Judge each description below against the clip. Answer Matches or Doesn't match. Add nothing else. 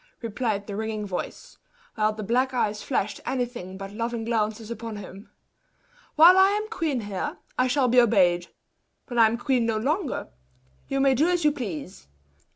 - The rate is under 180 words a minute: Matches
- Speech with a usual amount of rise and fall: Matches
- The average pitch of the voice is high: Matches